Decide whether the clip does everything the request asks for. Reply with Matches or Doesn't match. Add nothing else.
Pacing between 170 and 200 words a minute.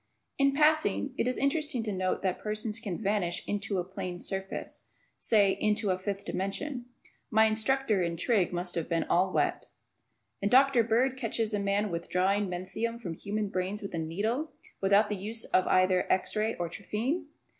Matches